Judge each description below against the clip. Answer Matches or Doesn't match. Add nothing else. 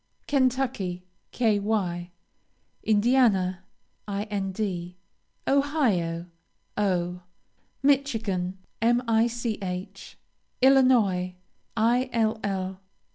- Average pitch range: Matches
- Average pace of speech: Doesn't match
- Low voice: Doesn't match